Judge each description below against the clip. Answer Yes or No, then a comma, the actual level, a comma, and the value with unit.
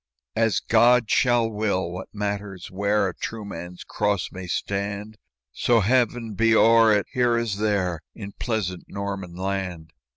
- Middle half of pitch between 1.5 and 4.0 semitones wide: Yes, average, 3.0 semitones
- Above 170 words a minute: No, average, 150 wpm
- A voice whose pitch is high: No, low, 105 Hz